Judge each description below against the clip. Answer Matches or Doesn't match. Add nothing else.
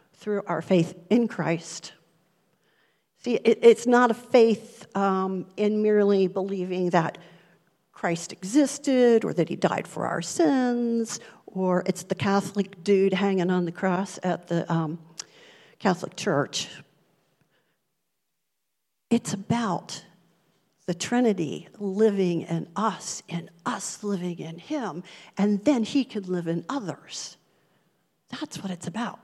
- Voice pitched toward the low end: Doesn't match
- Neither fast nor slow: Doesn't match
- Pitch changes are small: Doesn't match